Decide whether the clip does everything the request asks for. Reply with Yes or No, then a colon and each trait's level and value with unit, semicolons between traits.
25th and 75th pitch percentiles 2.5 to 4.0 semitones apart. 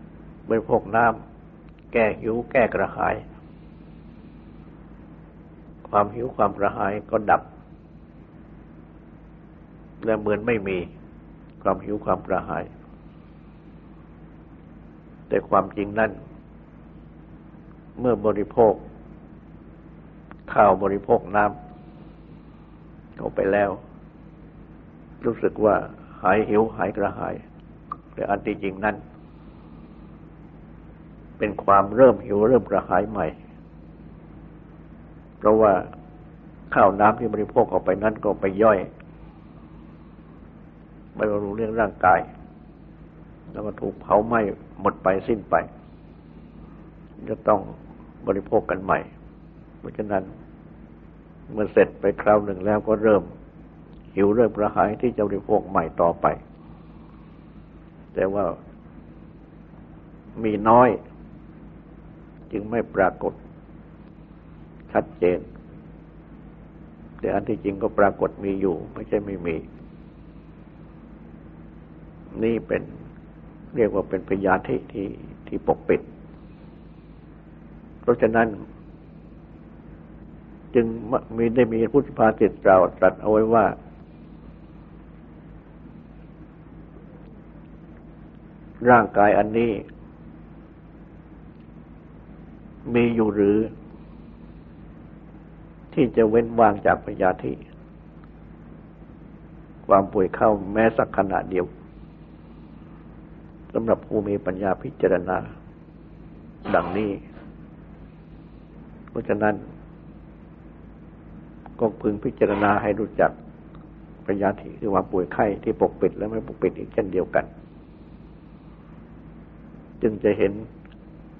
No: average, 5.1 semitones